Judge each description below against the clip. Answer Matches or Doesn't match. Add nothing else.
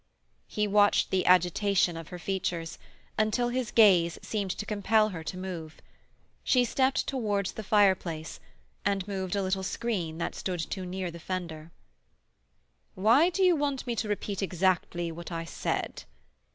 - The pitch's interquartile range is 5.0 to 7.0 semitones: Doesn't match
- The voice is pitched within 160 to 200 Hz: Matches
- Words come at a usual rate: Matches